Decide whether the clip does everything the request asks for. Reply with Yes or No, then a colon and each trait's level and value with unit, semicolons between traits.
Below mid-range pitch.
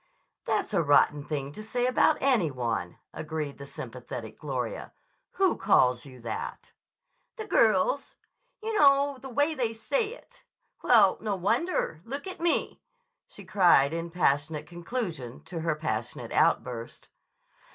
No: medium, 175 Hz